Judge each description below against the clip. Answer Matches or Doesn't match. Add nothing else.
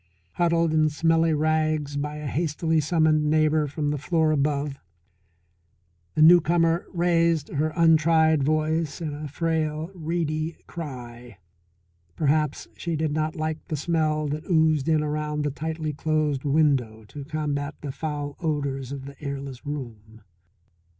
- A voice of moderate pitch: Matches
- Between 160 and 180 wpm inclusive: Doesn't match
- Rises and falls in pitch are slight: Matches